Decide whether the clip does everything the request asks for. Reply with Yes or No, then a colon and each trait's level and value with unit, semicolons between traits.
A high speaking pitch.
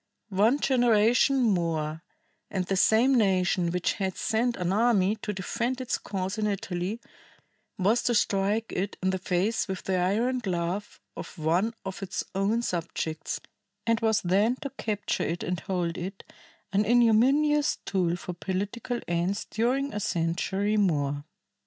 Yes: high, 200 Hz